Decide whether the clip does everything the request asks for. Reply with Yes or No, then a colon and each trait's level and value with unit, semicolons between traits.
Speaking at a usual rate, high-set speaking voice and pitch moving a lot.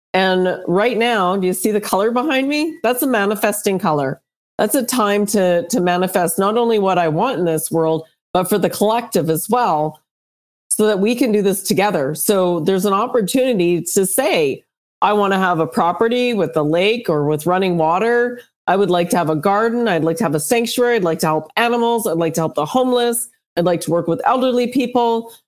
No: fast, 215 wpm; high, 200 Hz; wide, 5.7 semitones